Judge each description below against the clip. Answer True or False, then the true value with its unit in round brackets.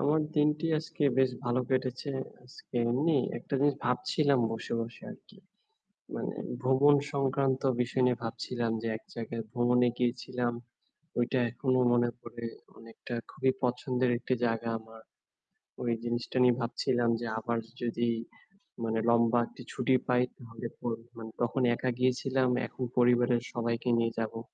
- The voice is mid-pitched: False (125 Hz)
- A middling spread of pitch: False (1.8 semitones)